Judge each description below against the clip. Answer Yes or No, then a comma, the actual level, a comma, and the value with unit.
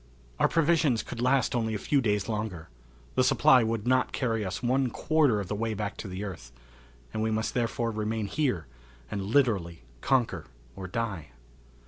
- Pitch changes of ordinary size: Yes, average, 3.8 semitones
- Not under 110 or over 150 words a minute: No, average, 175 wpm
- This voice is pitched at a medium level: No, low, 110 Hz